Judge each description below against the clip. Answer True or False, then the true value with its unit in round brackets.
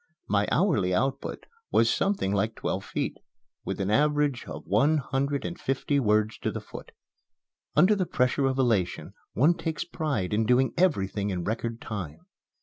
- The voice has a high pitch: False (125 Hz)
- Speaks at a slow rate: False (160 wpm)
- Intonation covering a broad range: True (6.1 semitones)